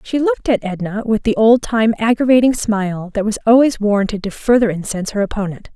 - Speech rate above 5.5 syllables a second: Yes, 6.0 syllables/s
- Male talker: No, female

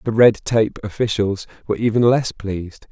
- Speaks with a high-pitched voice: No, low, 110 Hz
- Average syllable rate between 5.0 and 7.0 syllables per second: Yes, 5.2 syllables/s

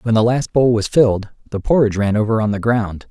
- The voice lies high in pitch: No, low, 110 Hz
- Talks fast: Yes, fast, 250 wpm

